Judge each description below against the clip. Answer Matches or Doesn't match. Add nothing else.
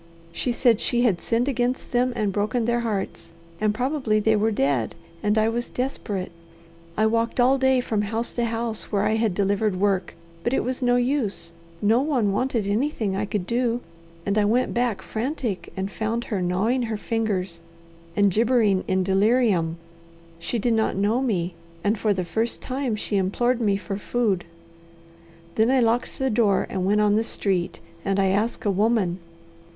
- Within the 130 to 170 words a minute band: Doesn't match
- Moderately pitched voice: Doesn't match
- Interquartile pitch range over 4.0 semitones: Doesn't match